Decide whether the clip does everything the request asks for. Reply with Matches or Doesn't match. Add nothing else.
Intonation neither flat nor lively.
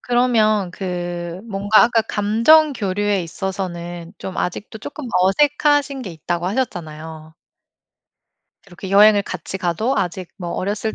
Matches